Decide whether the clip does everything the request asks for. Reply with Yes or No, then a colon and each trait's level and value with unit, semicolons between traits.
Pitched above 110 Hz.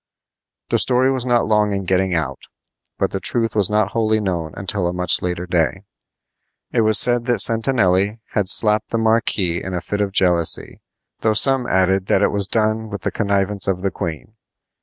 No: low, 100 Hz